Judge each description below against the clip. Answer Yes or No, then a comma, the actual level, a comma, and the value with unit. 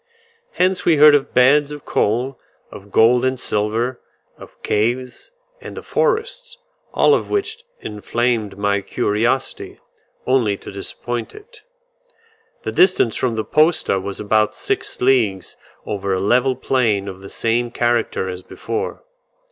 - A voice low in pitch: Yes, low, 120 Hz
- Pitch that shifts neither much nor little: Yes, average, 4.8 semitones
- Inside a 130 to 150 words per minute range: Yes, average, 140 wpm